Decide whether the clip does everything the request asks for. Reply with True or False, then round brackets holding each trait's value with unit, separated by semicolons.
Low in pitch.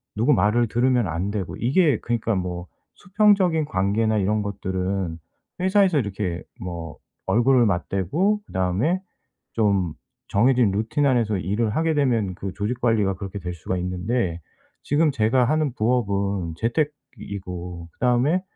True (110 Hz)